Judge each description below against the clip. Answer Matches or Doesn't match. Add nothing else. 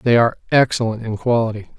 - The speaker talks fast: Doesn't match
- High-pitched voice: Doesn't match